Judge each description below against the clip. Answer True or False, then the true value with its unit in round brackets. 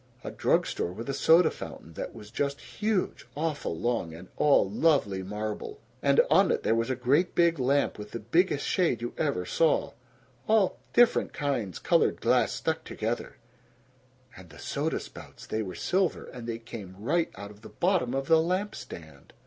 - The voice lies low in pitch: True (125 Hz)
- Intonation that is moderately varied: False (7.6 semitones)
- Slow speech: False (180 wpm)